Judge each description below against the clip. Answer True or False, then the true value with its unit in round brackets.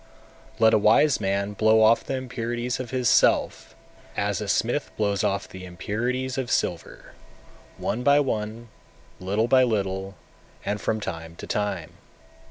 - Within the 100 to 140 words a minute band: False (155 wpm)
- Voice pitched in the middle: False (110 Hz)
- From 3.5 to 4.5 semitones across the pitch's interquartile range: True (3.8 semitones)